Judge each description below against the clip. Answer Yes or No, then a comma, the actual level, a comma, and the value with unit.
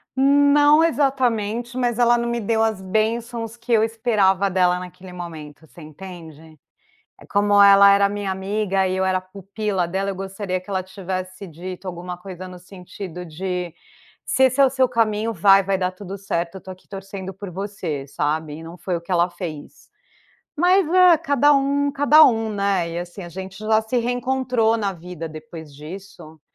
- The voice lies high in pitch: Yes, high, 195 Hz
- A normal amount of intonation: Yes, average, 4.1 semitones